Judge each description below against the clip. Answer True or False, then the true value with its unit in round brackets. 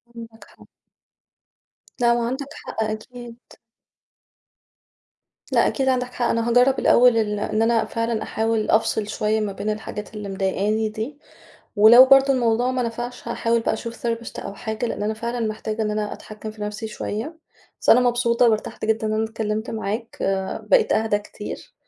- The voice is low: False (225 Hz)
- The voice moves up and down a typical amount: False (1.9 semitones)